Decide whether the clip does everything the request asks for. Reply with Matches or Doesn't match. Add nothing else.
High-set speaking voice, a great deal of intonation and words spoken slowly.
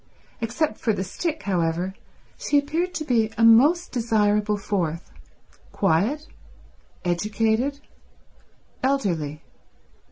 Matches